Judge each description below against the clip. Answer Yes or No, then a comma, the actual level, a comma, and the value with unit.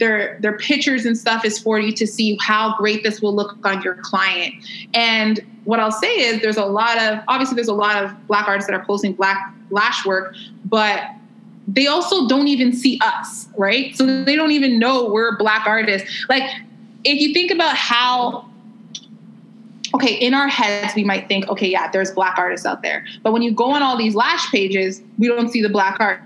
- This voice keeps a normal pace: No, fast, 210 wpm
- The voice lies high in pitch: Yes, high, 220 Hz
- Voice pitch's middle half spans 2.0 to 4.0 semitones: Yes, average, 2.9 semitones